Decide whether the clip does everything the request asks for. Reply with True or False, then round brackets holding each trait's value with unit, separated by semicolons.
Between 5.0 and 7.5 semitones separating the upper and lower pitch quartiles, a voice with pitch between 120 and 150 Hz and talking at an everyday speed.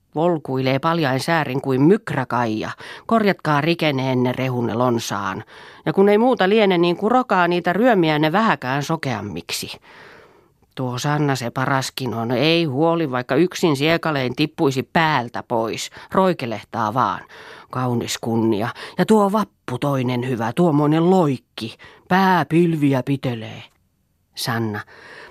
True (5.4 semitones; 140 Hz; 115 wpm)